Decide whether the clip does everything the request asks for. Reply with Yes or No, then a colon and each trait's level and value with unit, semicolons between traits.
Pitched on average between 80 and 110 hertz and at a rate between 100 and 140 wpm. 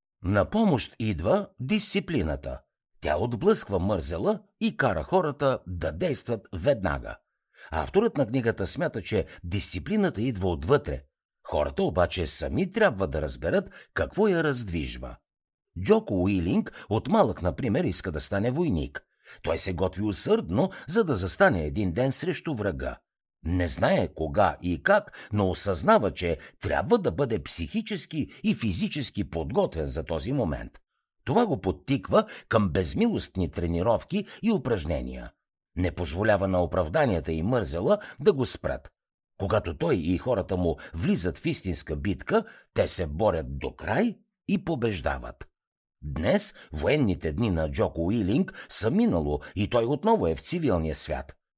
Yes: low, 100 Hz; average, 135 wpm